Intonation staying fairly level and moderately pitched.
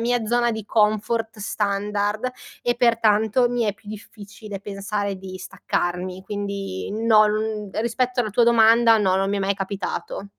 No: narrow, 2.3 semitones; high, 210 Hz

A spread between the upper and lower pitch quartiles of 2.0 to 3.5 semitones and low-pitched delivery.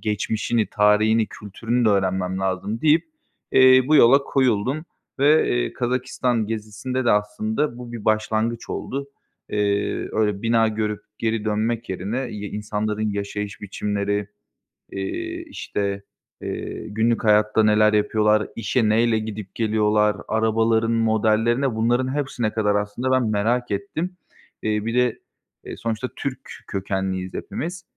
Yes: narrow, 2.4 semitones; low, 110 Hz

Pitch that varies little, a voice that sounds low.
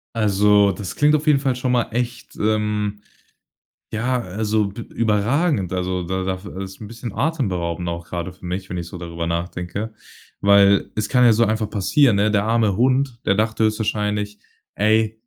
No: average, 3.5 semitones; low, 105 Hz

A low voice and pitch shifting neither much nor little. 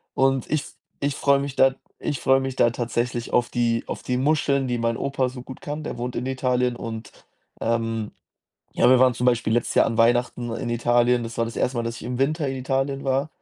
No: low, 125 Hz; narrow, 2.2 semitones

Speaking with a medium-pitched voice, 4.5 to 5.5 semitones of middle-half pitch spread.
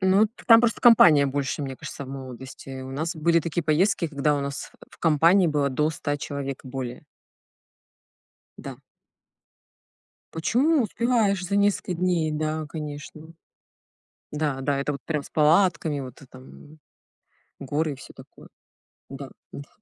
No: medium, 150 Hz; average, 4.0 semitones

